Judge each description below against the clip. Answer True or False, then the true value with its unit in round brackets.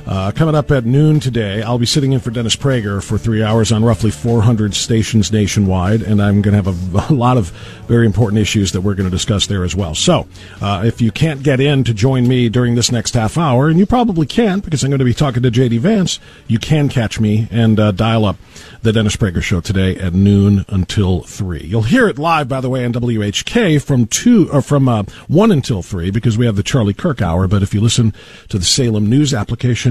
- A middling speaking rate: False (240 wpm)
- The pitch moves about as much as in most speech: True (4.5 semitones)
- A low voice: True (115 Hz)